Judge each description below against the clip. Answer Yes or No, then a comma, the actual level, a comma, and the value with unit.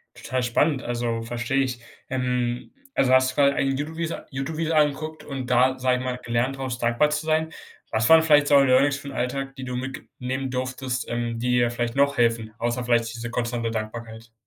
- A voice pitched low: Yes, low, 130 Hz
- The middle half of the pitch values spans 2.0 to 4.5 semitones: Yes, narrow, 2.5 semitones